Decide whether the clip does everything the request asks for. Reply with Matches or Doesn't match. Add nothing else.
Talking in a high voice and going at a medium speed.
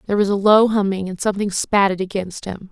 Doesn't match